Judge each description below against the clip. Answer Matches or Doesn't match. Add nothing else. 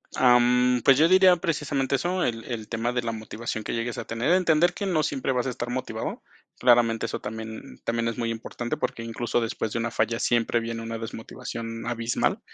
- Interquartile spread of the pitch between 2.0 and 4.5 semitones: Matches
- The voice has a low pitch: Matches